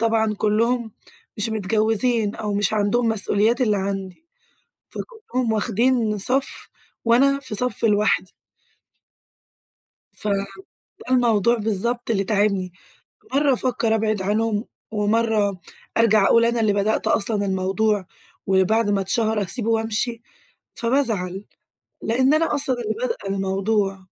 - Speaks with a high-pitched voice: Yes, high, 220 Hz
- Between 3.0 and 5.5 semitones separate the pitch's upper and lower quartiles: No, narrow, 2.6 semitones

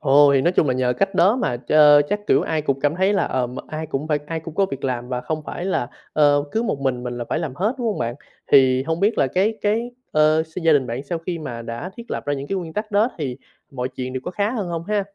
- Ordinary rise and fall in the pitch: No, wide, 6.3 semitones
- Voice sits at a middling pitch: Yes, medium, 155 Hz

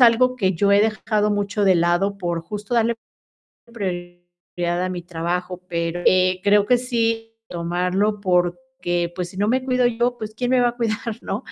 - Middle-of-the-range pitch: No, high, 200 Hz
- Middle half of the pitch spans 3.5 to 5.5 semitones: Yes, average, 4.6 semitones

